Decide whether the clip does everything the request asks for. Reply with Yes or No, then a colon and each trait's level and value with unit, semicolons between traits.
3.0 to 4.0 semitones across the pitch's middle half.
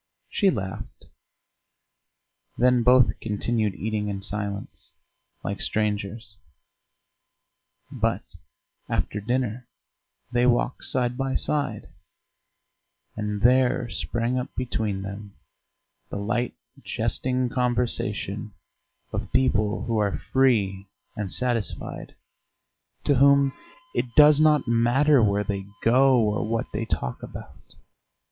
Yes: average, 3.5 semitones